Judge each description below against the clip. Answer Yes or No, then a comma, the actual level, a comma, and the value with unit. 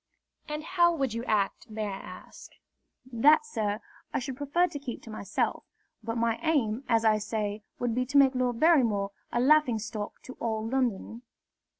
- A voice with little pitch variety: No, average, 4.3 semitones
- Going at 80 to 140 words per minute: No, average, 180 wpm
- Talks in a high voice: Yes, high, 235 Hz